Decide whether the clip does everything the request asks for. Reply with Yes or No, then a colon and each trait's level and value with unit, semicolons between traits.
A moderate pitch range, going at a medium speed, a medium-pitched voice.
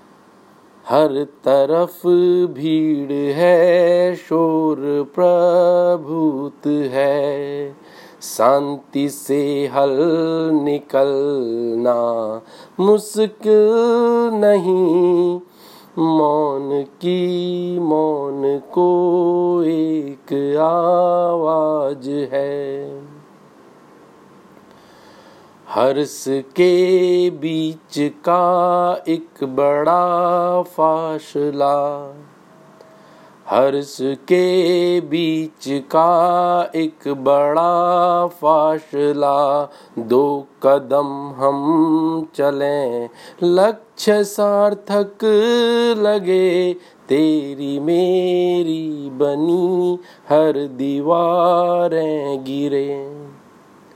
No: average, 3.8 semitones; slow, 50 wpm; medium, 160 Hz